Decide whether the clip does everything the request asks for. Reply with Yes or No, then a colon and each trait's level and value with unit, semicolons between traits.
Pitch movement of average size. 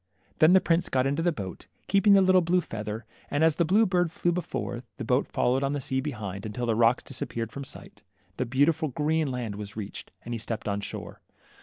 No: wide, 6.4 semitones